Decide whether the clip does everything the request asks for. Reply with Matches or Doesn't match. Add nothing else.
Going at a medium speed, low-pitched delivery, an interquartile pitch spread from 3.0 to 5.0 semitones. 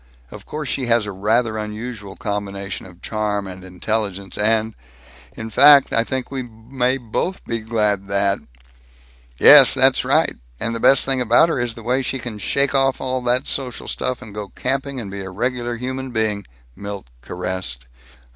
Matches